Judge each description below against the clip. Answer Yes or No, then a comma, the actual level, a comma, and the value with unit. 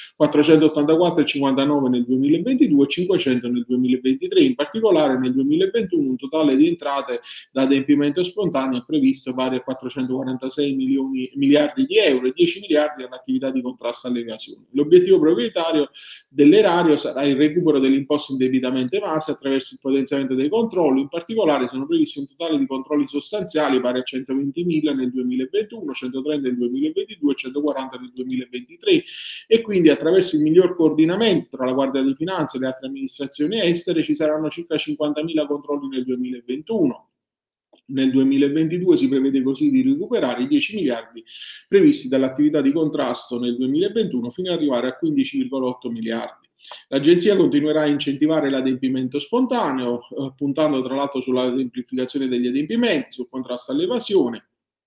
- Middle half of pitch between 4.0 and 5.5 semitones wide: Yes, average, 4.8 semitones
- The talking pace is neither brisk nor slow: Yes, average, 145 wpm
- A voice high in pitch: No, medium, 140 Hz